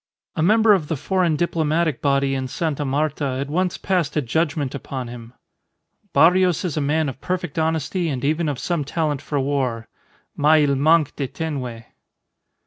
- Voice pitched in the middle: Yes, medium, 150 Hz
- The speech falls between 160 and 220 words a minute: Yes, average, 170 wpm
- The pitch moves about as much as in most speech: Yes, average, 3.4 semitones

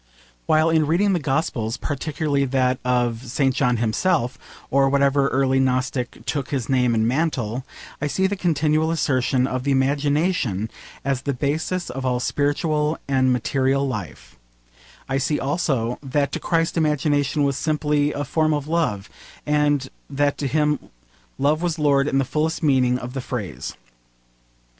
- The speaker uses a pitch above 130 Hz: Yes, medium, 140 Hz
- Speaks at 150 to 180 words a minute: Yes, average, 155 wpm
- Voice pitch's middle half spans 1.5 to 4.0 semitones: Yes, average, 2.9 semitones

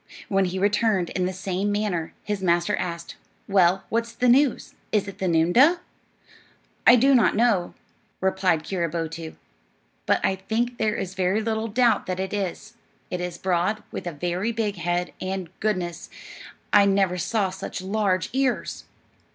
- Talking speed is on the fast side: No, average, 160 wpm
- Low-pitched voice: No, high, 190 Hz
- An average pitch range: Yes, average, 3.4 semitones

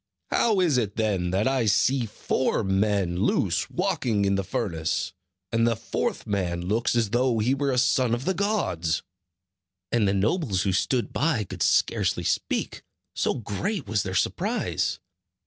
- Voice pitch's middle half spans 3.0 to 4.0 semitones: No, average, 4.9 semitones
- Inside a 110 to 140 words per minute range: No, average, 165 wpm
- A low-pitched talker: Yes, low, 110 Hz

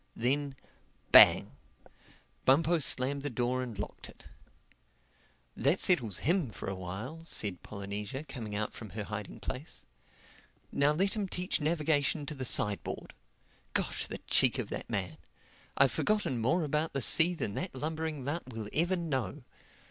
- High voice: No, medium, 140 Hz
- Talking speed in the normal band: Yes, average, 155 wpm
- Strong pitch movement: Yes, wide, 6.1 semitones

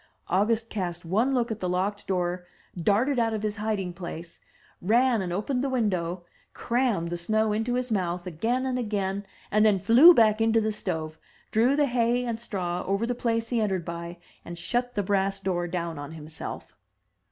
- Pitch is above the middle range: Yes, high, 205 Hz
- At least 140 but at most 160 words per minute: No, average, 185 wpm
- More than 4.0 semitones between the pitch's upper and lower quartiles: Yes, average, 4.7 semitones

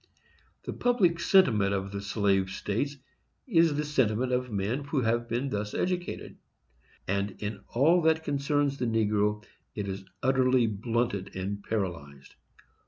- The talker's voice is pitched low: Yes, low, 115 Hz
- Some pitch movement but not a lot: No, wide, 5.9 semitones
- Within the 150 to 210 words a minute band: No, average, 140 wpm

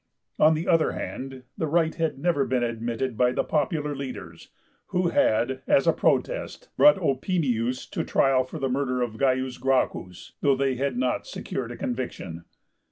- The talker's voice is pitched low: Yes, low, 130 Hz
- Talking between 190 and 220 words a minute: No, average, 165 wpm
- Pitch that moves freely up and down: No, average, 3.7 semitones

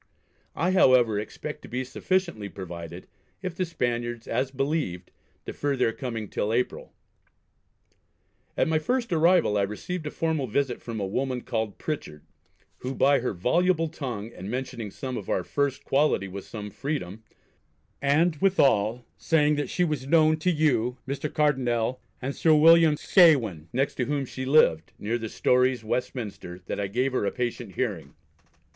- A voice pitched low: Yes, low, 130 Hz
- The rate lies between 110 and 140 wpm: No, average, 160 wpm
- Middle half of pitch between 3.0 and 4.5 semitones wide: No, wide, 5.5 semitones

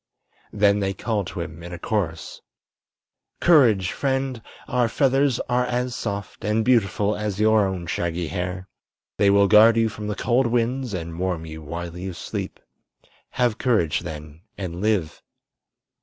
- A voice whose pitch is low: Yes, low, 100 Hz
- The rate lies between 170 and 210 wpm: No, average, 155 wpm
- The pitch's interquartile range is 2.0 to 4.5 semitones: No, average, 5.0 semitones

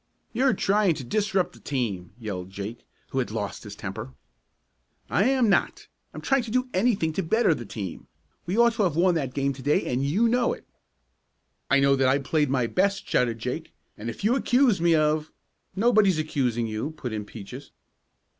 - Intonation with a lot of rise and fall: Yes, wide, 8.8 semitones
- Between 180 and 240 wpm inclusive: Yes, average, 195 wpm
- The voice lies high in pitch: No, medium, 150 Hz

